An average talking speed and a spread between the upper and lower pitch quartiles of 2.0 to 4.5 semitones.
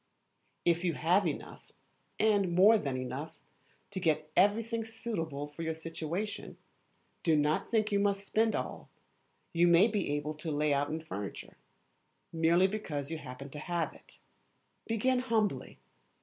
No: average, 150 wpm; average, 5.3 semitones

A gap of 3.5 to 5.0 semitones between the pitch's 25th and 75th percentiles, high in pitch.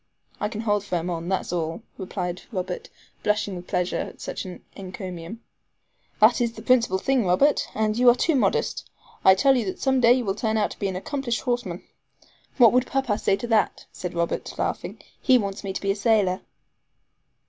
Yes: average, 4.5 semitones; high, 210 Hz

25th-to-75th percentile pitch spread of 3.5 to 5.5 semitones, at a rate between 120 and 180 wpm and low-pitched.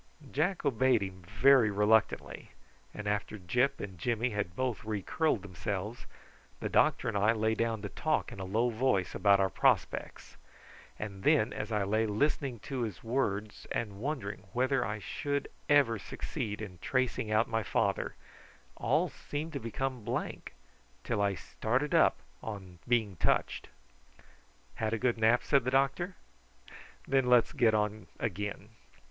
Yes: average, 3.9 semitones; average, 155 wpm; low, 110 Hz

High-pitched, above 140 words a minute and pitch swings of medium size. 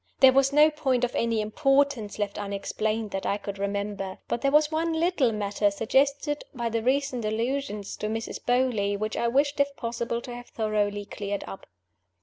Yes: high, 235 Hz; average, 180 wpm; average, 4.9 semitones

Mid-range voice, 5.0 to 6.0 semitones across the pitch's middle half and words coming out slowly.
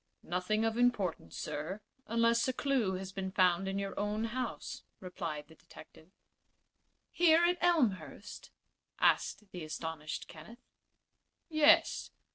No: high, 200 Hz; wide, 5.5 semitones; slow, 120 wpm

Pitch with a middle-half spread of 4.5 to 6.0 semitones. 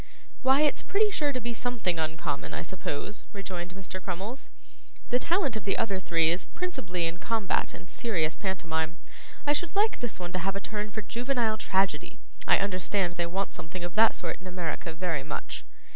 Yes: average, 5.0 semitones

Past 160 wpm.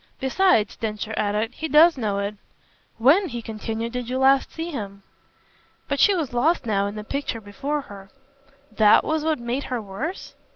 Yes: average, 175 wpm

